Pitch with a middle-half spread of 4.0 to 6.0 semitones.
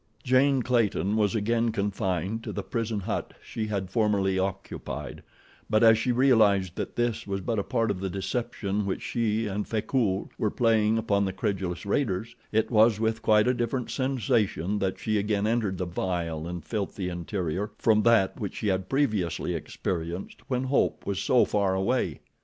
No: average, 3.2 semitones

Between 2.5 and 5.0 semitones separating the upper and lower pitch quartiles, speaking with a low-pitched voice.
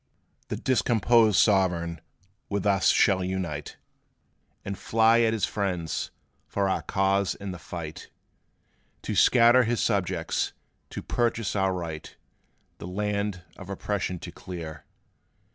Yes: average, 3.0 semitones; very low, 95 Hz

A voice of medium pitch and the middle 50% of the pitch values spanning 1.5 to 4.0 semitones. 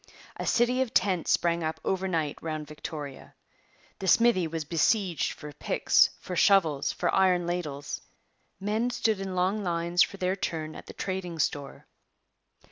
Yes: medium, 175 Hz; average, 3.5 semitones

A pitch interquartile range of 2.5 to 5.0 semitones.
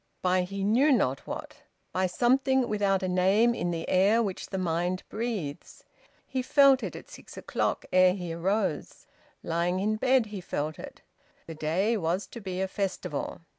Yes: average, 3.9 semitones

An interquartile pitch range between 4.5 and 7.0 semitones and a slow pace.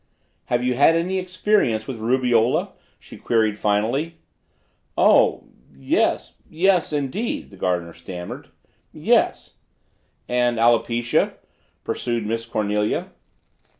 Yes: average, 5.0 semitones; slow, 105 wpm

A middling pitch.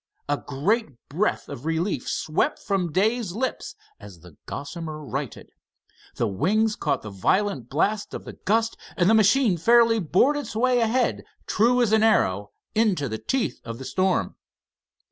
No: high, 195 Hz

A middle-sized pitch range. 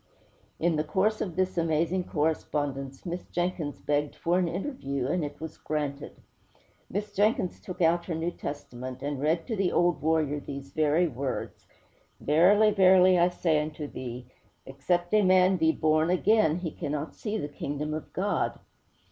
Yes: average, 3.8 semitones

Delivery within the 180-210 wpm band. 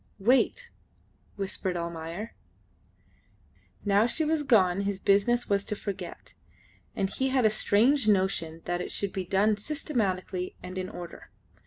No: average, 140 wpm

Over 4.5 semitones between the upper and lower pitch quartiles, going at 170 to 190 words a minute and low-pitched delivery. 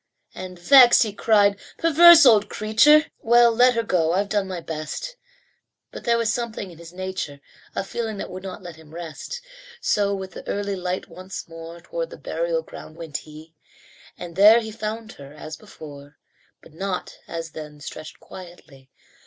No: wide, 5.6 semitones; average, 175 wpm; high, 190 Hz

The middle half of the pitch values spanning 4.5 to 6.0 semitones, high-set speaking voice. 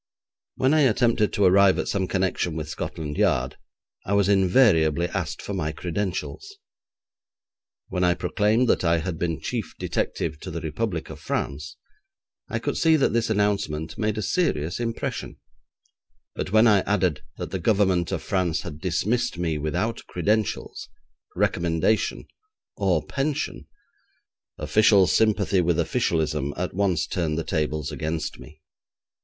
No: average, 4.9 semitones; very low, 90 Hz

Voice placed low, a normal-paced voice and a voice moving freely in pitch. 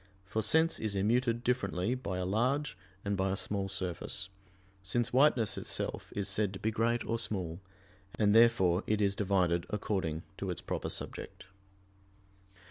No: low, 100 Hz; average, 155 wpm; average, 3.6 semitones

